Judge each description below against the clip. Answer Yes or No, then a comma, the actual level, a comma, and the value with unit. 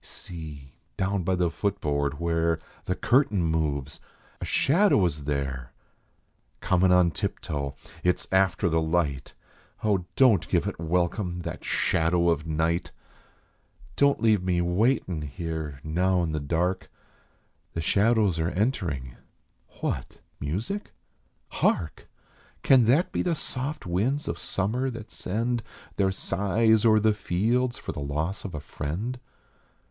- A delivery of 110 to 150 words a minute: Yes, average, 145 wpm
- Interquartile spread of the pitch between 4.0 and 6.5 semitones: Yes, average, 5.3 semitones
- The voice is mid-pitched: No, very low, 90 Hz